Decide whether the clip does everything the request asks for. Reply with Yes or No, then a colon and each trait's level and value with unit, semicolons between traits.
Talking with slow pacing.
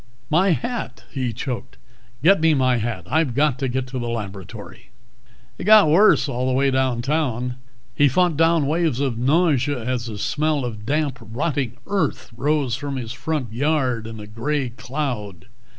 No: average, 165 wpm